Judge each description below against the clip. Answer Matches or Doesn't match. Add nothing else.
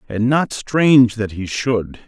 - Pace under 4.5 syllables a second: Matches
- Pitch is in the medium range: Doesn't match